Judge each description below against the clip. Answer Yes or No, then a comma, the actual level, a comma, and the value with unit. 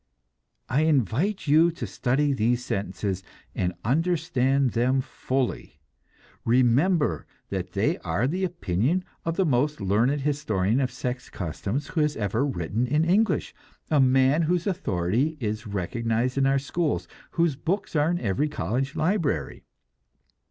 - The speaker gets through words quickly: No, average, 140 wpm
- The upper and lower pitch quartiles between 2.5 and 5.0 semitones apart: No, wide, 5.6 semitones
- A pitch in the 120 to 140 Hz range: Yes, low, 135 Hz